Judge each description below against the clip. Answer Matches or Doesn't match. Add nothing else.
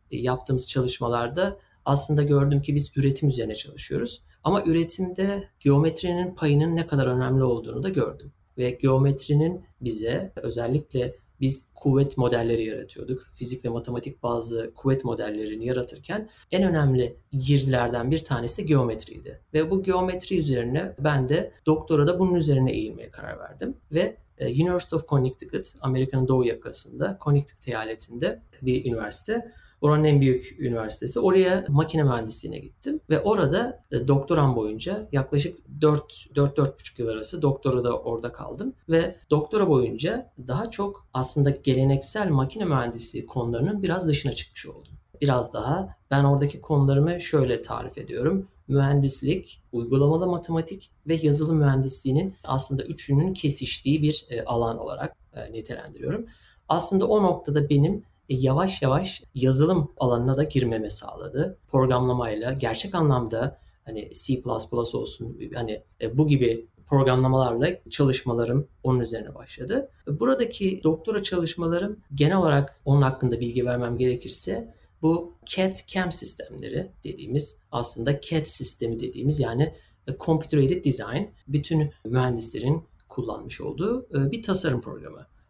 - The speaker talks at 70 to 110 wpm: Doesn't match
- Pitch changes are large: Doesn't match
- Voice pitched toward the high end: Doesn't match